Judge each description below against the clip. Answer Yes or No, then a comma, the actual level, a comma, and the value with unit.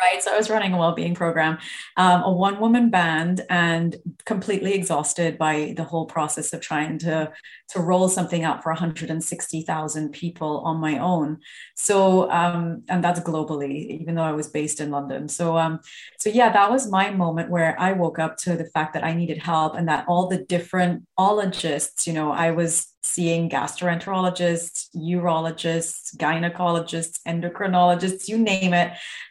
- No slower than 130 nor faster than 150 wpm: No, average, 165 wpm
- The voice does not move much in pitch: Yes, narrow, 2.1 semitones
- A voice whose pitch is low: No, medium, 170 Hz